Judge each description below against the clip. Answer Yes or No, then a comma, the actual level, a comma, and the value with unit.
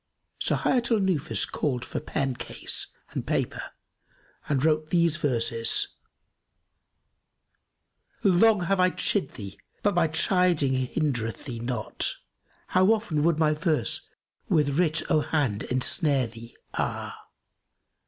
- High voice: No, medium, 155 Hz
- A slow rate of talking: Yes, slow, 125 wpm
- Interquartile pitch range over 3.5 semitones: Yes, wide, 5.5 semitones